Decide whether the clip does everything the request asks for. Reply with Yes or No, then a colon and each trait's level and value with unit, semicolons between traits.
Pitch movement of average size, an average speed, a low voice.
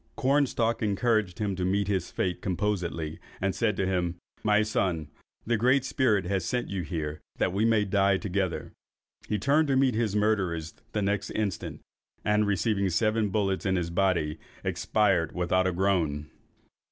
Yes: average, 3.2 semitones; average, 165 wpm; low, 100 Hz